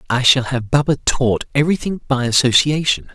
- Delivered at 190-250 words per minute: No, average, 150 wpm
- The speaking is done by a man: Yes, male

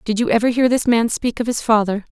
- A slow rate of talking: No, fast, 280 wpm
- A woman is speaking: Yes, female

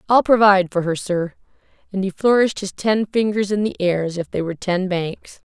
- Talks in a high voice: Yes, high, 195 Hz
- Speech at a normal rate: No, fast, 220 wpm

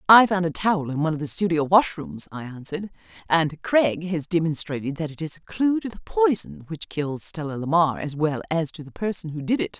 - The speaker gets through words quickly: Yes, fast, 225 wpm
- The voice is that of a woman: Yes, female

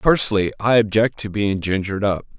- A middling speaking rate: Yes, average, 175 wpm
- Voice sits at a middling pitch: No, low, 105 Hz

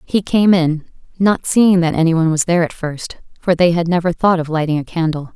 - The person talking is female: Yes, female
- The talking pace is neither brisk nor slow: No, fast, 235 wpm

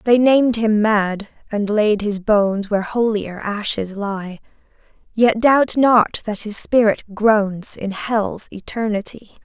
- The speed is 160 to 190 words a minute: No, average, 140 wpm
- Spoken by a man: No, female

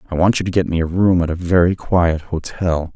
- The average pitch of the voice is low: Yes, very low, 85 Hz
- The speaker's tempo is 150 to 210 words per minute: No, fast, 265 wpm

